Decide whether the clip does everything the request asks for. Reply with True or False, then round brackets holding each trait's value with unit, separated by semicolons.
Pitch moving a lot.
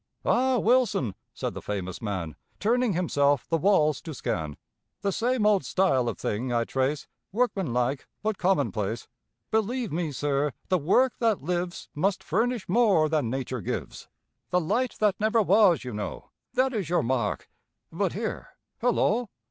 True (8.7 semitones)